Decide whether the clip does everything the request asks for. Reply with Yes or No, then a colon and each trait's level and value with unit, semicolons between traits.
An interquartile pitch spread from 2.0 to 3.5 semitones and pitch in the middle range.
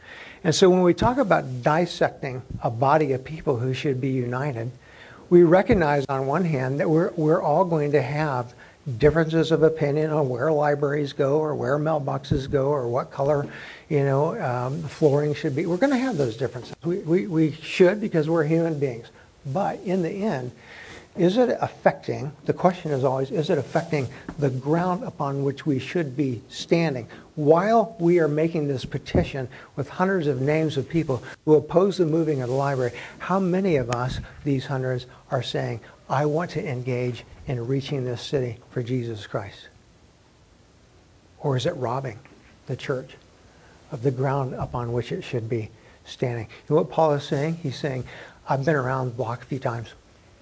No: average, 3.9 semitones; medium, 145 Hz